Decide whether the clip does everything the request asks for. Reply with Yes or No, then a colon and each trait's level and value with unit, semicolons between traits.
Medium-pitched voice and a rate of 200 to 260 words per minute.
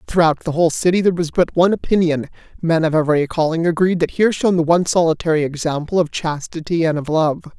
Yes: medium, 165 Hz; fast, 205 wpm